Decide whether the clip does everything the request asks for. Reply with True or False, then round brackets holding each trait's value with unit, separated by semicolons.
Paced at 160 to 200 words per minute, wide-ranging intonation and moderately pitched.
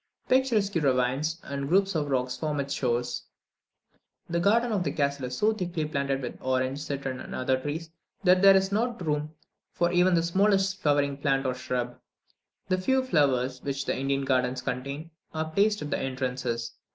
True (175 wpm; 5.8 semitones; 145 Hz)